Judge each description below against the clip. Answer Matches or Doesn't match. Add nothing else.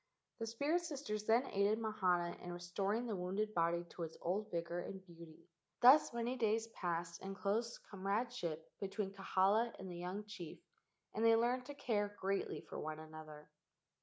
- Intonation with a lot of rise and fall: Doesn't match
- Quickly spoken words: Doesn't match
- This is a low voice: Doesn't match